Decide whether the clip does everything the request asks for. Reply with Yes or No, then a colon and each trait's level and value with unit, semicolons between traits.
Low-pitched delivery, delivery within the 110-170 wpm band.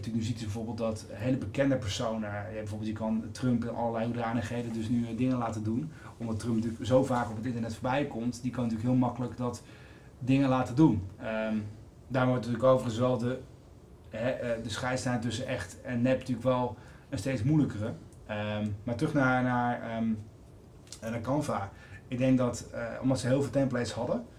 No: low, 120 Hz; average, 185 wpm